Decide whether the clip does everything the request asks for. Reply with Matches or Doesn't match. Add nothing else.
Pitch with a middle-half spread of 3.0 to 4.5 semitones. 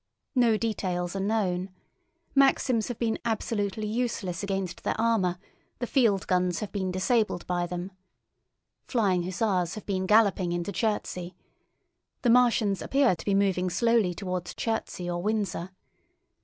Matches